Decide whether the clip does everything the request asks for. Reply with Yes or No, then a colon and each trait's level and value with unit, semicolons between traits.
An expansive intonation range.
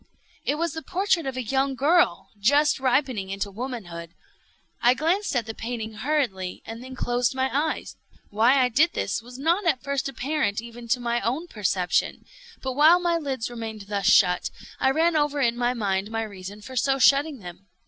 No: average, 4.7 semitones